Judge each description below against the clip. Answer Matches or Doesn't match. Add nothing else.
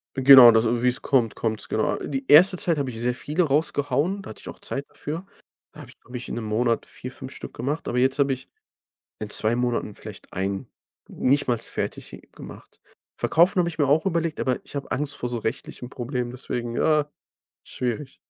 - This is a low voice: Matches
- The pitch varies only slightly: Doesn't match